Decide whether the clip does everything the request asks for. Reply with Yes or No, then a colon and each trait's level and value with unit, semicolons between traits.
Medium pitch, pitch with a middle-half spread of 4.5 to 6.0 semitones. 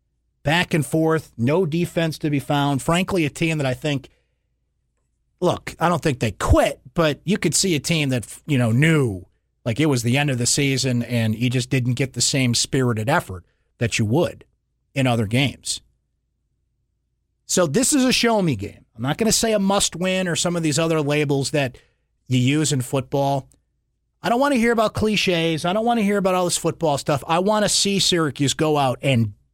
Yes: medium, 145 Hz; average, 5.2 semitones